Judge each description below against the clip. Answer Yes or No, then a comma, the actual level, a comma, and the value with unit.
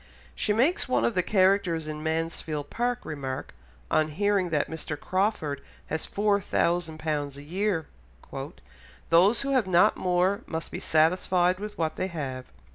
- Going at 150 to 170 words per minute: Yes, average, 155 wpm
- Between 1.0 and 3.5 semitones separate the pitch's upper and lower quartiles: No, average, 4.4 semitones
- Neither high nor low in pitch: Yes, medium, 175 Hz